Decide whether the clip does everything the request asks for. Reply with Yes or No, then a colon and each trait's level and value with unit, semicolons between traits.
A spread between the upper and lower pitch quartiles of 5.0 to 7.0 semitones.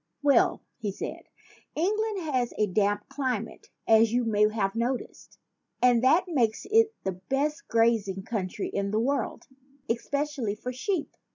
Yes: average, 5.3 semitones